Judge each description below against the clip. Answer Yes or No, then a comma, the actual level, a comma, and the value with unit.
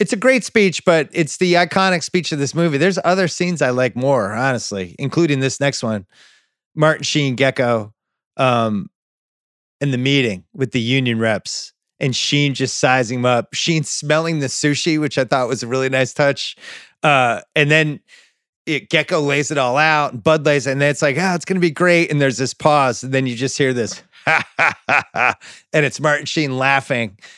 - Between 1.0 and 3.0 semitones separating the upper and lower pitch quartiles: No, average, 3.5 semitones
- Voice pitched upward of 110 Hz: Yes, medium, 140 Hz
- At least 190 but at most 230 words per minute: Yes, average, 200 wpm